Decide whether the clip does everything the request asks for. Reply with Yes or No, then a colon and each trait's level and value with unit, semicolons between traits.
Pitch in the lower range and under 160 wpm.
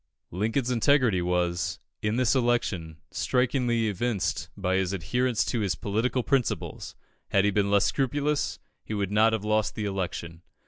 Yes: low, 110 Hz; average, 150 wpm